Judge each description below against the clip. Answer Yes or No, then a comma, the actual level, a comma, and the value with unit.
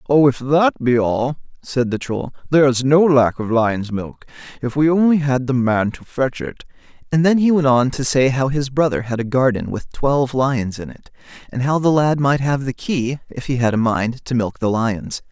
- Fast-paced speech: Yes, fast, 225 wpm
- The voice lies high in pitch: No, low, 130 Hz